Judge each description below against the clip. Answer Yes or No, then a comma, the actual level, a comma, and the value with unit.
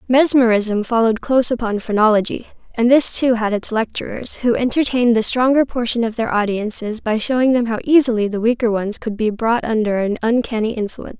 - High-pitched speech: Yes, high, 230 Hz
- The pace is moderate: Yes, average, 180 wpm